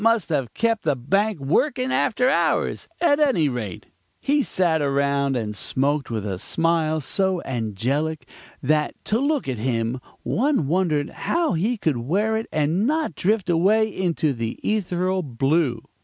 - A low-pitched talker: No, medium, 160 Hz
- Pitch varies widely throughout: Yes, wide, 8.1 semitones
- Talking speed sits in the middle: Yes, average, 155 wpm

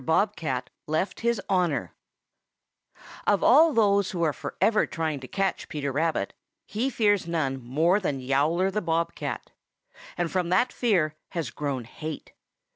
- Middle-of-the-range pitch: Yes, medium, 170 Hz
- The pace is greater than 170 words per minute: No, average, 150 wpm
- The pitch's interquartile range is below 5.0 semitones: No, average, 5.3 semitones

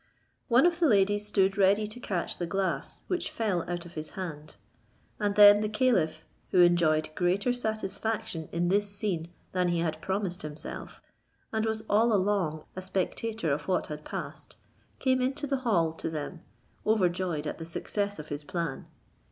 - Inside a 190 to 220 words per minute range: No, average, 170 wpm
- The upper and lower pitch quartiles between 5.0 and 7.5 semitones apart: No, average, 4.3 semitones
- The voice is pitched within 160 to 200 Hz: Yes, high, 190 Hz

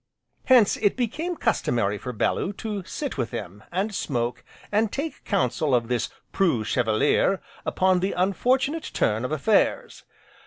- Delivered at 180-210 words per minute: No, average, 145 wpm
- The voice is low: No, medium, 185 Hz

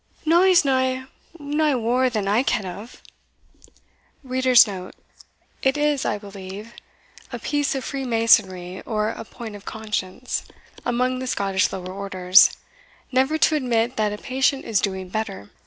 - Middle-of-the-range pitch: No, high, 230 Hz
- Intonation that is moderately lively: Yes, average, 4.7 semitones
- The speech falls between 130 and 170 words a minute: Yes, average, 140 wpm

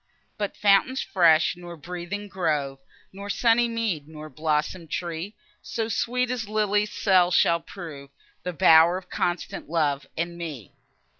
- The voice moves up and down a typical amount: Yes, average, 4.4 semitones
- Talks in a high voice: No, medium, 175 Hz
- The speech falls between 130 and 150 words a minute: Yes, average, 140 wpm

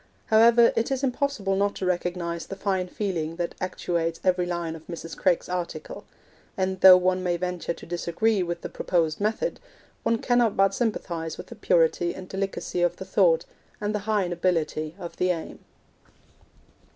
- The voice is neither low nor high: Yes, medium, 180 Hz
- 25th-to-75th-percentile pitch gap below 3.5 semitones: Yes, average, 2.8 semitones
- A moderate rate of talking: Yes, average, 170 wpm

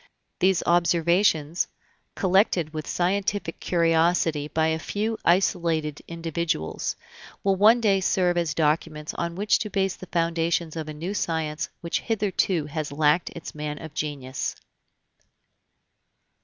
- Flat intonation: No, average, 3.2 semitones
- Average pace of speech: No, slow, 130 wpm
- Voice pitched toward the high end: No, medium, 170 Hz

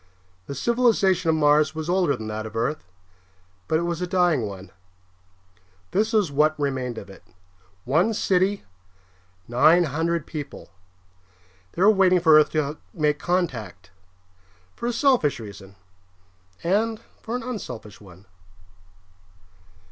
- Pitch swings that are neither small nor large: No, wide, 6.4 semitones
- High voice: No, medium, 155 Hz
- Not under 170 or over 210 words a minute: No, slow, 135 wpm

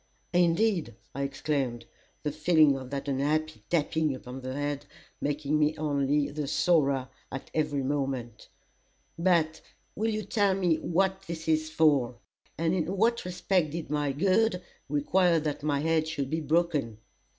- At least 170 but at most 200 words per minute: No, average, 150 wpm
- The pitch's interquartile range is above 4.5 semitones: No, average, 3.4 semitones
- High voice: No, medium, 155 Hz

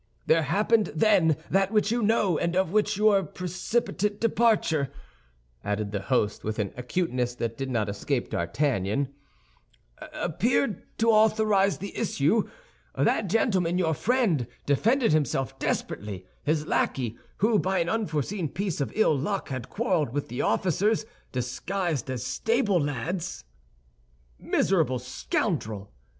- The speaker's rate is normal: No, slow, 130 wpm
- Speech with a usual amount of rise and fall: No, wide, 8.1 semitones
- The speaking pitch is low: No, medium, 170 Hz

